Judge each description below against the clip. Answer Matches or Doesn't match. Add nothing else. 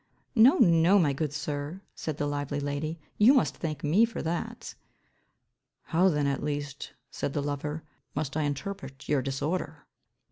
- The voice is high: Doesn't match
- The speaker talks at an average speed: Matches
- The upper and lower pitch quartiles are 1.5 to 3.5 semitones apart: Matches